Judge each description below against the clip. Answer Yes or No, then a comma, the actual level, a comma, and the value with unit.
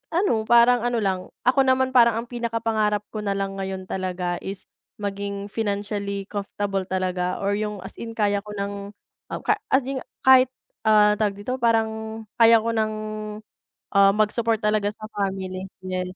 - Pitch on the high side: Yes, high, 210 Hz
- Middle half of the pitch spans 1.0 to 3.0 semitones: Yes, narrow, 2.6 semitones